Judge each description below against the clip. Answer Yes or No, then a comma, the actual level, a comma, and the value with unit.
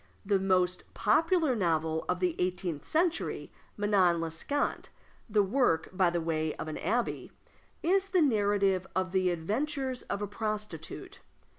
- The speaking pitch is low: No, high, 195 Hz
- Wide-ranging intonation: Yes, wide, 5.8 semitones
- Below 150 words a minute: Yes, average, 140 wpm